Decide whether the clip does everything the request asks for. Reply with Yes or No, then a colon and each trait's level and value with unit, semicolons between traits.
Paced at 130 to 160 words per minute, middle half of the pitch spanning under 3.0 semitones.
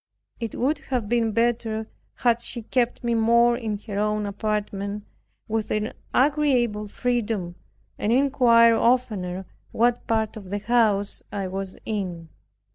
Yes: slow, 135 wpm; narrow, 2.6 semitones